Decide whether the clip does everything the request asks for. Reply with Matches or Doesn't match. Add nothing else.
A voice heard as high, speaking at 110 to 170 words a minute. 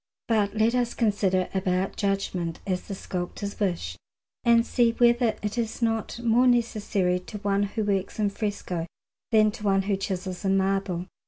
Matches